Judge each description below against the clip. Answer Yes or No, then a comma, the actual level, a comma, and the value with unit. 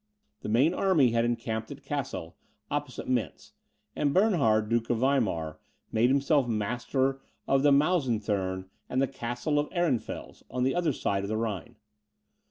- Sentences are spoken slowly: No, average, 155 wpm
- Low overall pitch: Yes, low, 120 Hz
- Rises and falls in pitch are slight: No, average, 4.1 semitones